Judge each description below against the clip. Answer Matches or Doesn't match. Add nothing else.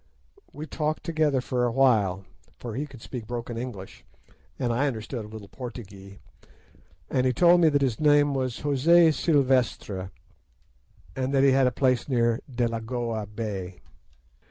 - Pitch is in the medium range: Doesn't match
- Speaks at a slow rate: Doesn't match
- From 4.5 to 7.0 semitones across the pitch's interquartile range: Doesn't match